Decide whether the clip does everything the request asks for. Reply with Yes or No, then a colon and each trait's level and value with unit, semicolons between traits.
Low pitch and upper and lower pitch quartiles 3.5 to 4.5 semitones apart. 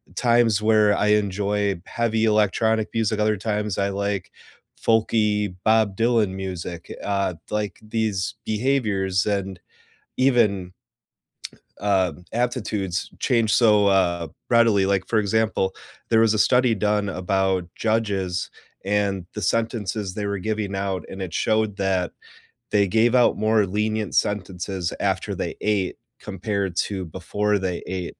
No: low, 105 Hz; narrow, 2.4 semitones